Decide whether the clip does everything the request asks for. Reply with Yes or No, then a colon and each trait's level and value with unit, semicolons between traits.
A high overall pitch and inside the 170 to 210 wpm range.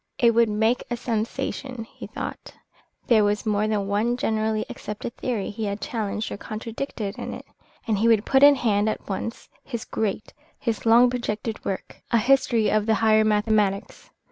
Yes: high, 220 Hz; average, 175 wpm